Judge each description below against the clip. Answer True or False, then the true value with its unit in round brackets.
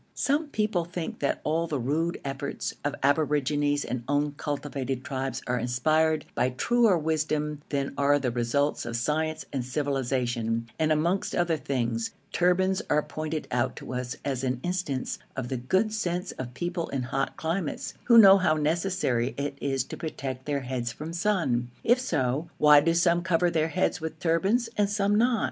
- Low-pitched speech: False (150 Hz)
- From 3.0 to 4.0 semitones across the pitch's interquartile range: False (4.7 semitones)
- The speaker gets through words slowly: False (175 wpm)